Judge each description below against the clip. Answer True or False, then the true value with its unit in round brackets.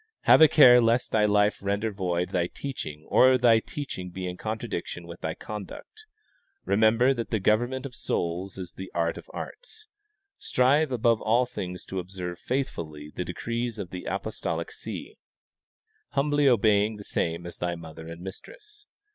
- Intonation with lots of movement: True (5.7 semitones)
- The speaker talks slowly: False (165 wpm)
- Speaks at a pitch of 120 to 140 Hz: False (105 Hz)